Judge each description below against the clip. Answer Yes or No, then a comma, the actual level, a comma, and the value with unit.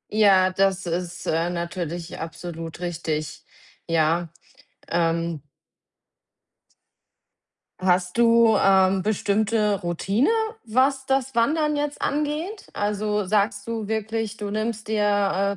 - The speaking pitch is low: No, high, 200 Hz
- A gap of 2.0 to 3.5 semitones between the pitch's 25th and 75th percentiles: No, average, 4.2 semitones